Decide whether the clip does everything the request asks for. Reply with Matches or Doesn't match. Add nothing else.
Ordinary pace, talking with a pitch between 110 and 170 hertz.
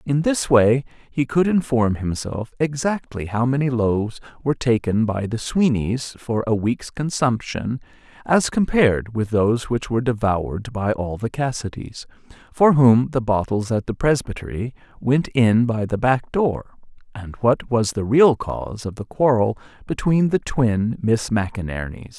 Matches